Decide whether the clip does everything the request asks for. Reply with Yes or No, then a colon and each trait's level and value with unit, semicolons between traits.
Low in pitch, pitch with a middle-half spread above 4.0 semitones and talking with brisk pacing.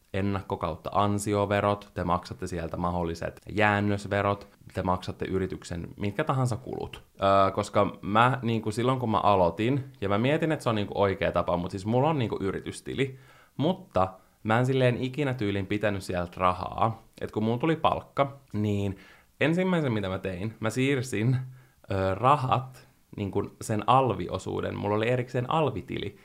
Yes: low, 105 Hz; average, 4.7 semitones; fast, 160 wpm